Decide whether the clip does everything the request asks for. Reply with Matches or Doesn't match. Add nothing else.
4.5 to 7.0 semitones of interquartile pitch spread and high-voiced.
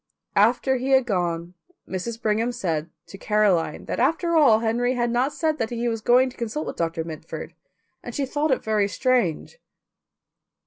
Matches